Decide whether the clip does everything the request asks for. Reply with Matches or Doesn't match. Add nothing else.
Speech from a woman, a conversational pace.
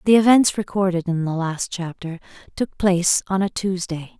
Matches